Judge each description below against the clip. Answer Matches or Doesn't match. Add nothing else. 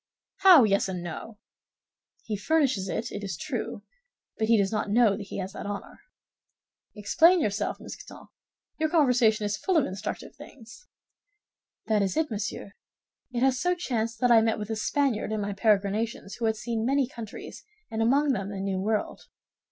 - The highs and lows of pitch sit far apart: Doesn't match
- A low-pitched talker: Doesn't match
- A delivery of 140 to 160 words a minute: Doesn't match